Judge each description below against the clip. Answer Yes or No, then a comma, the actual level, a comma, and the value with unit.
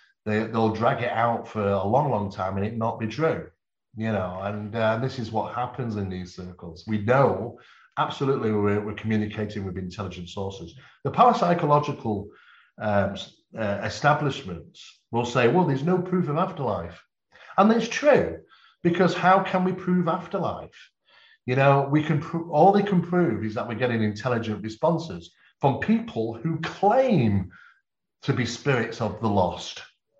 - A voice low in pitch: Yes, low, 115 Hz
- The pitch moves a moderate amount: No, wide, 7.4 semitones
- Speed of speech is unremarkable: Yes, average, 165 wpm